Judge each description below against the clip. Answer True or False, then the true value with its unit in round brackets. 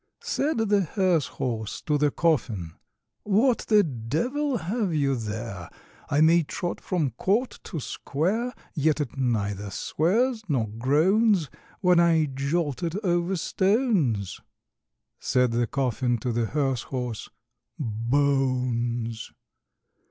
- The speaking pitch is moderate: True (145 Hz)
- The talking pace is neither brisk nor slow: False (120 wpm)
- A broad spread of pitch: True (7.4 semitones)